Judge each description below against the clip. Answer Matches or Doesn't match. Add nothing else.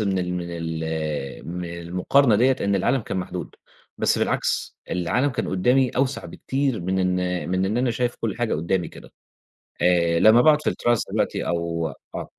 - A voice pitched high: Doesn't match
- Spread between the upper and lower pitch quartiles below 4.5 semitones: Doesn't match